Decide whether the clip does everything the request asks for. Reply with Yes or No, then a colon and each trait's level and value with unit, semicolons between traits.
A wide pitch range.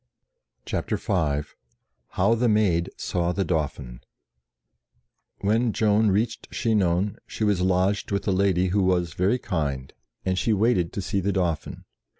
No: average, 3.2 semitones